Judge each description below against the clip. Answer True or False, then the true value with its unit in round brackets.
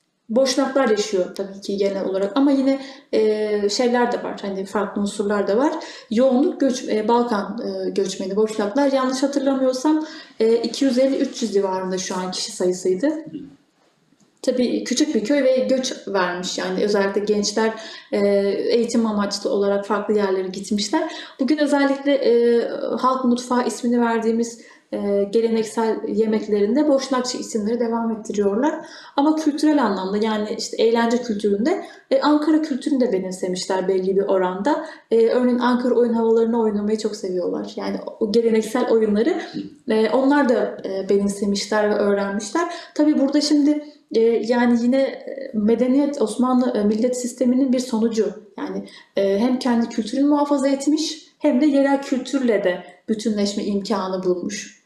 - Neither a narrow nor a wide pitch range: True (4.8 semitones)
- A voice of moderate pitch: False (235 Hz)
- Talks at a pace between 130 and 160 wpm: True (135 wpm)